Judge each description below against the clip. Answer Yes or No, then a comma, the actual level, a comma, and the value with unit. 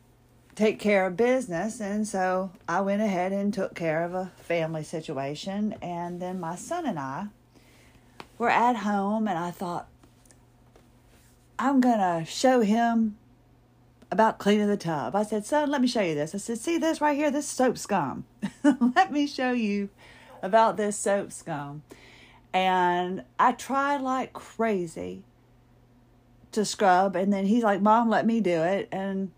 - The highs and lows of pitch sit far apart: Yes, wide, 6.0 semitones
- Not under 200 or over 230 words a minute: No, average, 160 wpm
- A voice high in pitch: Yes, high, 195 Hz